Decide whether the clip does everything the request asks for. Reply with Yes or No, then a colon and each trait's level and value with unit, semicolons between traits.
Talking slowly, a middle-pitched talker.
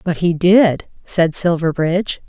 Yes: slow, 130 wpm; medium, 170 Hz